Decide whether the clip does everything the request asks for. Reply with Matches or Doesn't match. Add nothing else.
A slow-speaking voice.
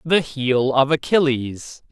Matches